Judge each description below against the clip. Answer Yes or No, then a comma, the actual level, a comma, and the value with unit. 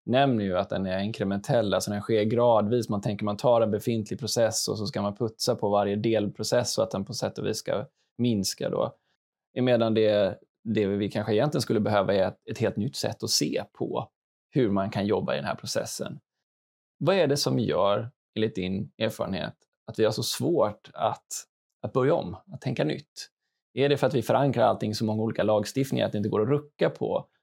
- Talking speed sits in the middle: No, fast, 210 wpm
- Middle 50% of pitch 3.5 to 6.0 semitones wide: No, average, 2.7 semitones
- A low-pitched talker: Yes, low, 110 Hz